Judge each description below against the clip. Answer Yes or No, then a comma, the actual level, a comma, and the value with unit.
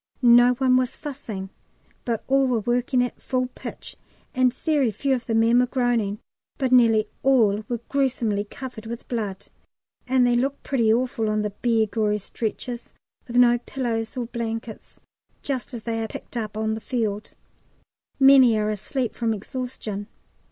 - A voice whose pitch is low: No, high, 235 Hz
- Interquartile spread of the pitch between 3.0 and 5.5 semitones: No, narrow, 2.6 semitones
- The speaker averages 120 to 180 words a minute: Yes, average, 165 wpm